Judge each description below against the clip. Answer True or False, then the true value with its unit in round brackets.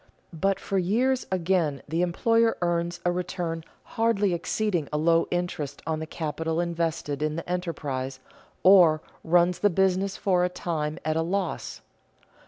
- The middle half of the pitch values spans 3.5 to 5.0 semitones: False (2.8 semitones)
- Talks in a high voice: False (175 Hz)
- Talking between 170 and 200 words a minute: False (150 wpm)